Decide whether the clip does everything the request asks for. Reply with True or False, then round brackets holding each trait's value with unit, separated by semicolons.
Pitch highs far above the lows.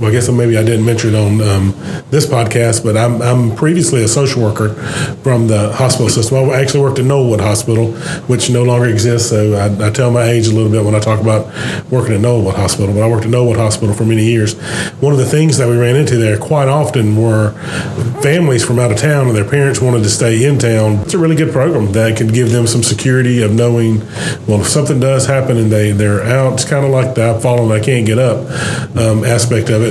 False (3.1 semitones)